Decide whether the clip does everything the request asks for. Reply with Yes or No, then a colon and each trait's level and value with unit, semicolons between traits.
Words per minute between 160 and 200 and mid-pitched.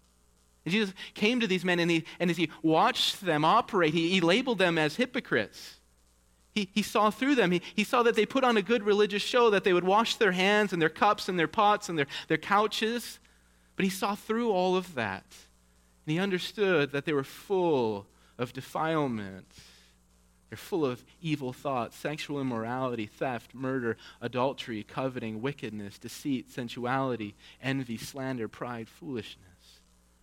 Yes: average, 170 wpm; medium, 150 Hz